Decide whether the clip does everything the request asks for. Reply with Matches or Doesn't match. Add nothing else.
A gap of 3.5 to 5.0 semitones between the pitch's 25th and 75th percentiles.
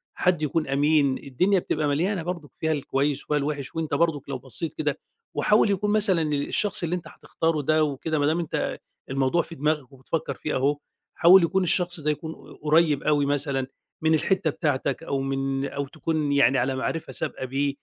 Doesn't match